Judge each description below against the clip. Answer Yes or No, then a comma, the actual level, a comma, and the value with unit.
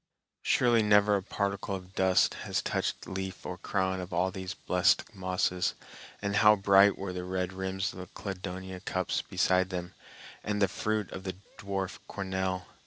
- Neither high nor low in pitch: No, very low, 95 Hz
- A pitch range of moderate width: No, narrow, 1.4 semitones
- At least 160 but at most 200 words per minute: Yes, average, 170 wpm